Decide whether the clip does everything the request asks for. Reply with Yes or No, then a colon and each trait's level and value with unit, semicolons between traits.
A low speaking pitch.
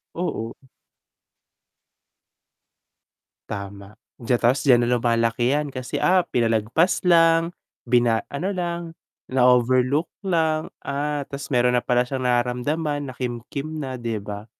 Yes: low, 130 Hz